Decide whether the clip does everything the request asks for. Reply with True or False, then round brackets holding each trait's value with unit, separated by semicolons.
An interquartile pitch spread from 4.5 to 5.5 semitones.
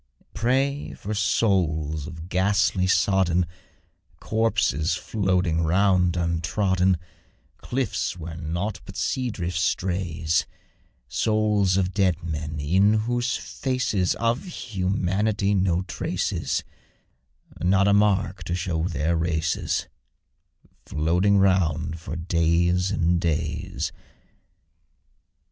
False (3.3 semitones)